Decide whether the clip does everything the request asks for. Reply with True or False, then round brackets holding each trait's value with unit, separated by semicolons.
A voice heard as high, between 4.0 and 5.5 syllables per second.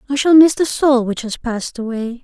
True (255 Hz; 5.4 syllables/s)